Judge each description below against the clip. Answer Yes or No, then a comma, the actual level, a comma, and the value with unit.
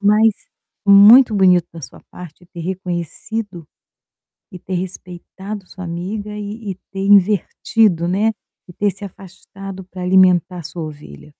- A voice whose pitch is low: No, medium, 185 Hz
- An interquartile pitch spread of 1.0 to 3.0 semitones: Yes, narrow, 2.6 semitones